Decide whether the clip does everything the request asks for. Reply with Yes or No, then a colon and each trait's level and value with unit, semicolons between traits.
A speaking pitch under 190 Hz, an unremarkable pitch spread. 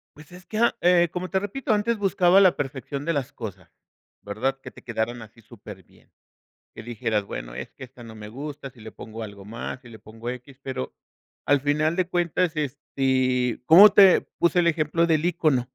No: low, 135 Hz; wide, 6.7 semitones